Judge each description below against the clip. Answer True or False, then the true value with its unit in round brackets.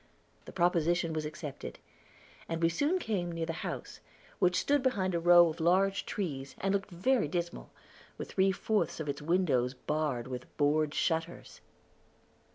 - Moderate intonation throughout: True (3.6 semitones)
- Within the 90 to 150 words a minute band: False (160 wpm)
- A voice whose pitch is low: False (170 Hz)